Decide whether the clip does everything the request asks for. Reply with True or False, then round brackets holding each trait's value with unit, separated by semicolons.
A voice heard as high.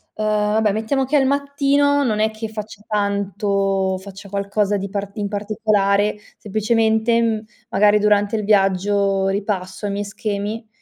True (210 Hz)